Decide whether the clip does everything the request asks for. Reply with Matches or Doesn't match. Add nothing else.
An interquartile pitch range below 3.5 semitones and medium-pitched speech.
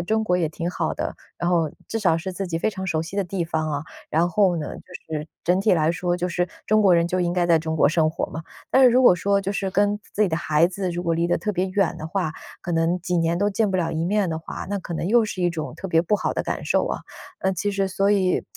Matches